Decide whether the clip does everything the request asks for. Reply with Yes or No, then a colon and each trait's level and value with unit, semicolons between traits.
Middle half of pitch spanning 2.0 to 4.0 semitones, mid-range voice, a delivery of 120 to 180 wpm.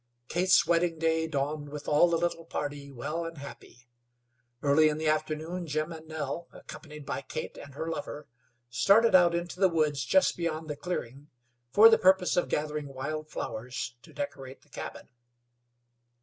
Yes: average, 3.0 semitones; medium, 155 Hz; average, 165 wpm